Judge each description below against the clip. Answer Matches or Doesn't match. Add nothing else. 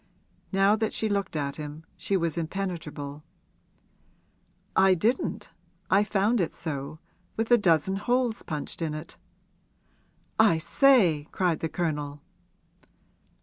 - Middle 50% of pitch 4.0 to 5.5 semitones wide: Matches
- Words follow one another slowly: Matches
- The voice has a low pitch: Doesn't match